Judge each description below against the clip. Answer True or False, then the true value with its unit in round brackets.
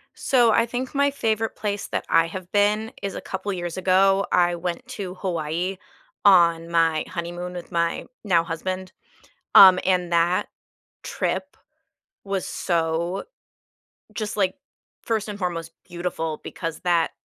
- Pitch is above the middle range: False (180 Hz)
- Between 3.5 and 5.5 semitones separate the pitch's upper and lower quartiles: False (3.0 semitones)